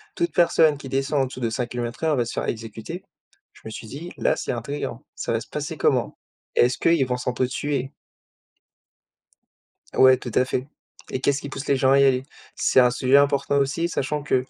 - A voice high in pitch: No, low, 135 Hz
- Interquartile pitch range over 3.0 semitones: No, narrow, 2.5 semitones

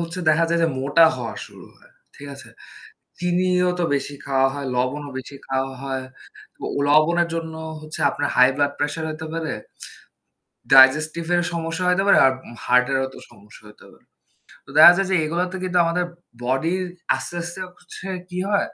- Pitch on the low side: No, medium, 160 Hz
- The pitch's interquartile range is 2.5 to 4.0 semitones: No, average, 4.4 semitones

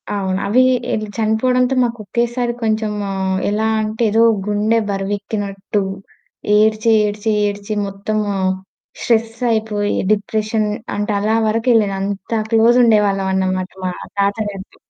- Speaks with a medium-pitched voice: No, high, 215 Hz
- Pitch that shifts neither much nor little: No, narrow, 2.0 semitones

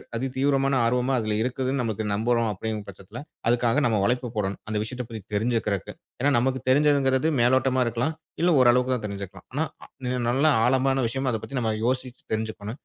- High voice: No, low, 125 Hz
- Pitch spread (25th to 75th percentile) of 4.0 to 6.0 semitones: No, average, 3.1 semitones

